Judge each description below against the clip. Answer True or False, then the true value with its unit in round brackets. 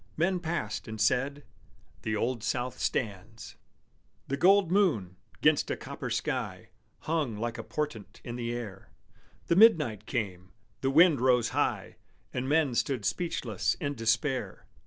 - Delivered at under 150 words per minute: True (140 wpm)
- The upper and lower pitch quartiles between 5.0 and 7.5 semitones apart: True (5.6 semitones)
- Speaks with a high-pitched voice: False (125 Hz)